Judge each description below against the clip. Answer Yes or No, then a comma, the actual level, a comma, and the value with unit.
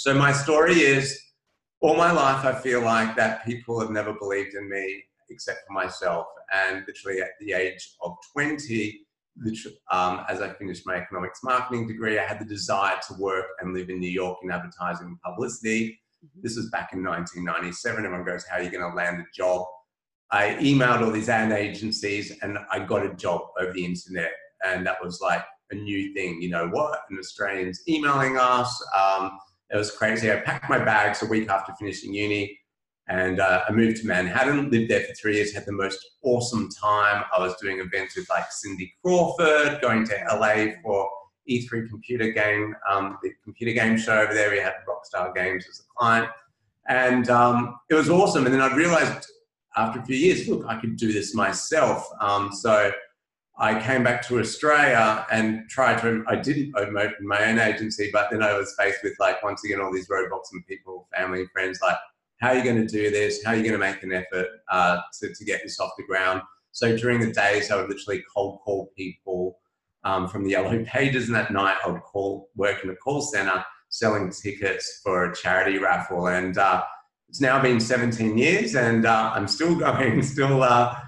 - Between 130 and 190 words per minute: No, average, 200 wpm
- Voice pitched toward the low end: Yes, low, 105 Hz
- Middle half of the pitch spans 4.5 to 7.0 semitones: No, average, 4.0 semitones